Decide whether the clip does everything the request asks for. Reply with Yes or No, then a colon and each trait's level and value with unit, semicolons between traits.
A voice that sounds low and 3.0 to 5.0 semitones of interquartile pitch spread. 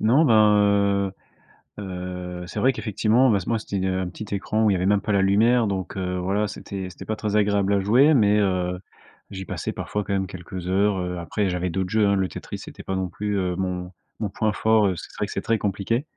No: low, 100 Hz; narrow, 2.4 semitones